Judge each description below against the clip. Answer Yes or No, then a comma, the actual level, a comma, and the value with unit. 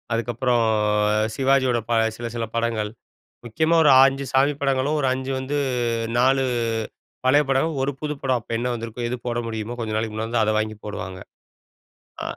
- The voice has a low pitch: Yes, low, 120 Hz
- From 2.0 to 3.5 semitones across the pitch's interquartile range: Yes, average, 3.0 semitones